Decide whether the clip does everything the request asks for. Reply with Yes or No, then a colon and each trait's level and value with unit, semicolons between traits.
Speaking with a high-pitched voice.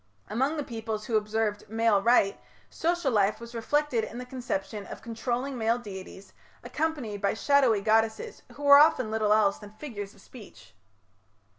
Yes: high, 225 Hz